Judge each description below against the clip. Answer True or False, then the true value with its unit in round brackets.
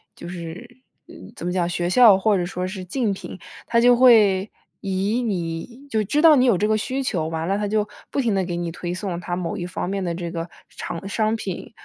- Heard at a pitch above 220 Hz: False (195 Hz)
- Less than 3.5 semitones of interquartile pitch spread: False (4.3 semitones)